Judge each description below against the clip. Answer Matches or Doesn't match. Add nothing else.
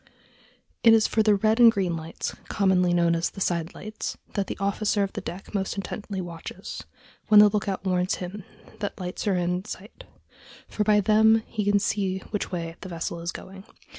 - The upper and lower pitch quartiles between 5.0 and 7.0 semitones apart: Doesn't match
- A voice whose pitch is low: Doesn't match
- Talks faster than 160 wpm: Matches